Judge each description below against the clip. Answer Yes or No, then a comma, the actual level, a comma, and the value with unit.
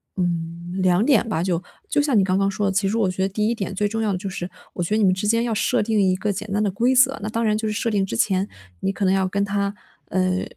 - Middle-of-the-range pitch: No, high, 200 Hz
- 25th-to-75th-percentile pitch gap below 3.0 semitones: Yes, narrow, 2.5 semitones